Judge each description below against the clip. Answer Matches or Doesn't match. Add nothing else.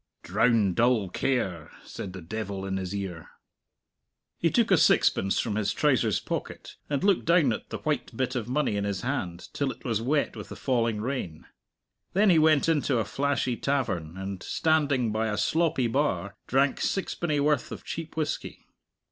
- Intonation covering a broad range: Matches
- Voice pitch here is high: Doesn't match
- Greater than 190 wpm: Doesn't match